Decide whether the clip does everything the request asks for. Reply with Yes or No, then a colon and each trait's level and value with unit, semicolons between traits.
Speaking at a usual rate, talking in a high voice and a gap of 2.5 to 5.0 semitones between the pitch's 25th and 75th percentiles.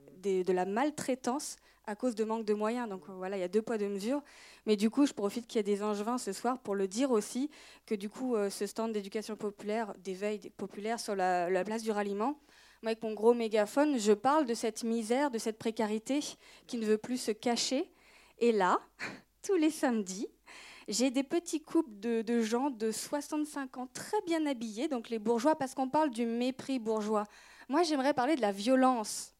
Yes: average, 210 wpm; high, 230 Hz; average, 4.4 semitones